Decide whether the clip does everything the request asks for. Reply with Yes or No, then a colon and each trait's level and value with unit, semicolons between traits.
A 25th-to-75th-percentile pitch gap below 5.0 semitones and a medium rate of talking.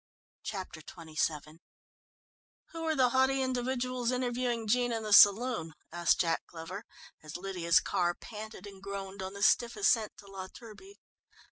No: average, 5.3 semitones; average, 145 wpm